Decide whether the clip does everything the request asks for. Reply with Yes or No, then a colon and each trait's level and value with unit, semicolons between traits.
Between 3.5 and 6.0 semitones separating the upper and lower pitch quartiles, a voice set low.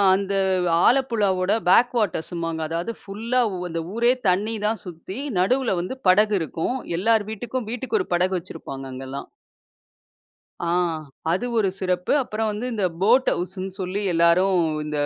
No: average, 4.4 semitones; high, 195 Hz